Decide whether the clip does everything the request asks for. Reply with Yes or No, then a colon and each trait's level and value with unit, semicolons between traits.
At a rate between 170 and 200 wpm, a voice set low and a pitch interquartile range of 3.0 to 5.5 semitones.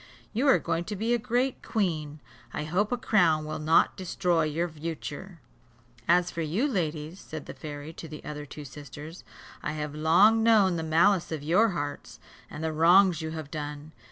No: average, 185 wpm; medium, 165 Hz; average, 3.9 semitones